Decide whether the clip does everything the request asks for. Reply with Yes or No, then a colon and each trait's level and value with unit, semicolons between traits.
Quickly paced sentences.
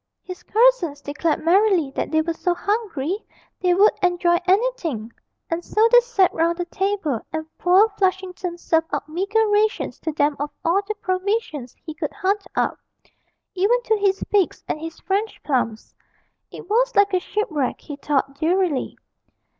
No: average, 160 wpm